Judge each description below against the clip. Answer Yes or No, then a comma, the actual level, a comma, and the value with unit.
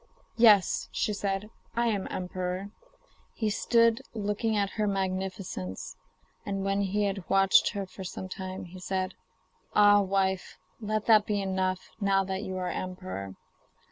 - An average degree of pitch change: No, narrow, 1.7 semitones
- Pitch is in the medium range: No, high, 195 Hz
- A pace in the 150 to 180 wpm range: No, average, 140 wpm